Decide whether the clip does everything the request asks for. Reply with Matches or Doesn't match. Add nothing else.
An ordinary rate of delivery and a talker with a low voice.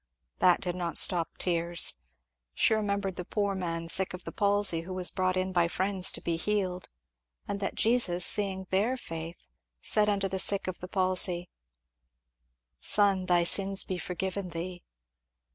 Doesn't match